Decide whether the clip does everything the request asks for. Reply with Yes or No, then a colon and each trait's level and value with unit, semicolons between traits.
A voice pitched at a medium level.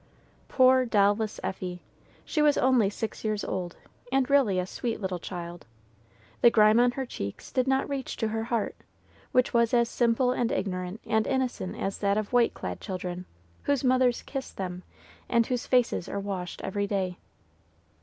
No: high, 220 Hz